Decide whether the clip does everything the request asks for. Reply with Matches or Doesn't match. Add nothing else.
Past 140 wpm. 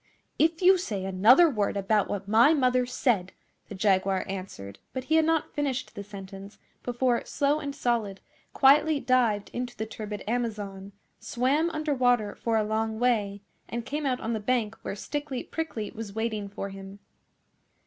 Matches